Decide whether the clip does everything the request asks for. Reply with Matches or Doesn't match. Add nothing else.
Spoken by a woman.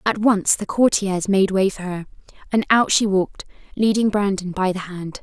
Matches